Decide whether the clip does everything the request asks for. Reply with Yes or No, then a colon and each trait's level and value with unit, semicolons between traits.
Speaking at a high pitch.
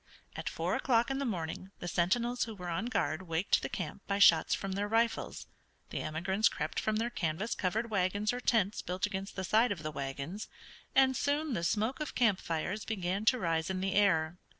Yes: high, 200 Hz